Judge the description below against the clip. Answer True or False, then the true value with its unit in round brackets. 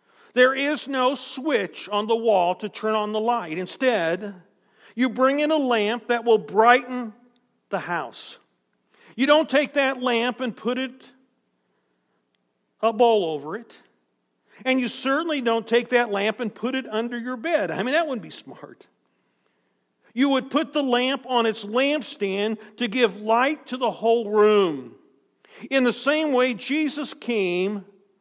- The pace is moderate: True (160 wpm)